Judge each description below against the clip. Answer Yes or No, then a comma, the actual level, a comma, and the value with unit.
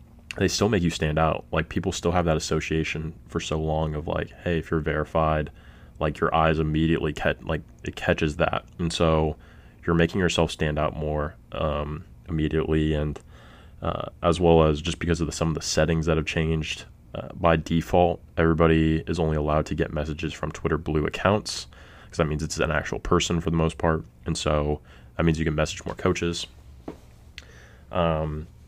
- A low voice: Yes, very low, 80 Hz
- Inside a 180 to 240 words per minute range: Yes, average, 190 wpm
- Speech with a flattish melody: Yes, narrow, 1.5 semitones